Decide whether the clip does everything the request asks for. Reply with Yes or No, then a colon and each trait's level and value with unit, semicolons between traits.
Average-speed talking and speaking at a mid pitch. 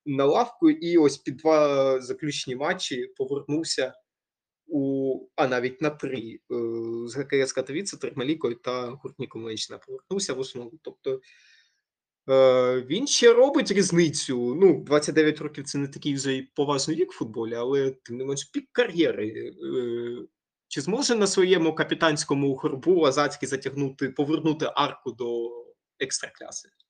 Yes: average, 130 wpm; medium, 150 Hz